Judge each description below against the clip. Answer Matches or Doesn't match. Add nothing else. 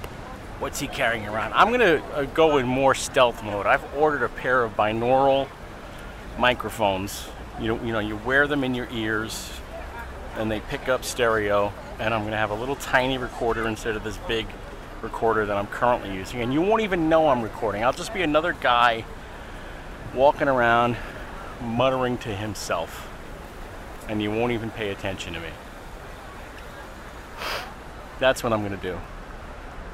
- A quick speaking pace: Doesn't match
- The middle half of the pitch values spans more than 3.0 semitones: Matches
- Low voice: Matches